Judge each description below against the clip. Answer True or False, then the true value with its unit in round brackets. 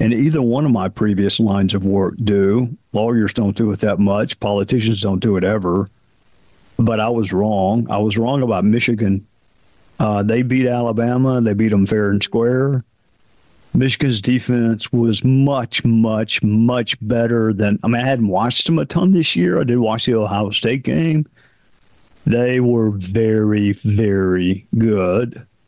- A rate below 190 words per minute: True (165 wpm)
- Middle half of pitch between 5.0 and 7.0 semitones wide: False (2.8 semitones)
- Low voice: True (115 Hz)